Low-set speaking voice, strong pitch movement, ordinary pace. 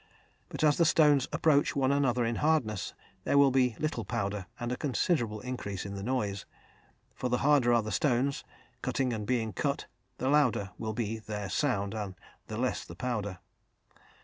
No: low, 120 Hz; average, 4.6 semitones; average, 175 wpm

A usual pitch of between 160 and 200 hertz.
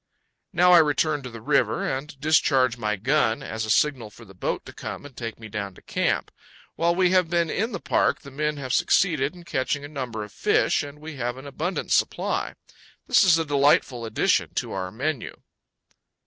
No: medium, 140 Hz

